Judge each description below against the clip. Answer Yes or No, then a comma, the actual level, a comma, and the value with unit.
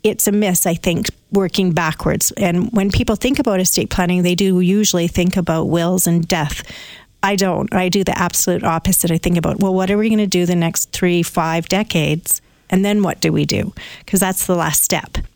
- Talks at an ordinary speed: No, fast, 215 wpm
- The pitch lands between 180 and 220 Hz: Yes, medium, 185 Hz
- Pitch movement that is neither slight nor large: No, narrow, 2.2 semitones